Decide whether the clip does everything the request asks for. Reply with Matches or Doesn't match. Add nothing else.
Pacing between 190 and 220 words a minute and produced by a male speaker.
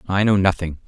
Matches